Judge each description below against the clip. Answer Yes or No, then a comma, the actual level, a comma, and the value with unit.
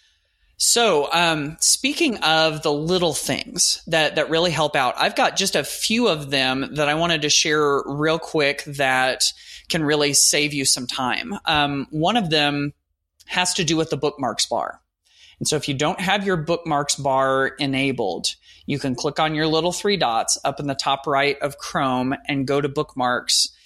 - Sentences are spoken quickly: No, average, 185 wpm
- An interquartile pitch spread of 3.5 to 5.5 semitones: No, average, 3.0 semitones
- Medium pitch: Yes, medium, 150 Hz